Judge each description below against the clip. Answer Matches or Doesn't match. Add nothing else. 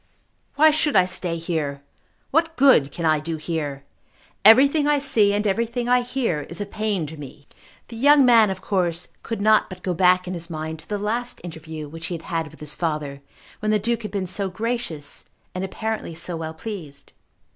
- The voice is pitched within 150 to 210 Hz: Matches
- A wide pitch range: Matches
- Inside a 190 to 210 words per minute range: Matches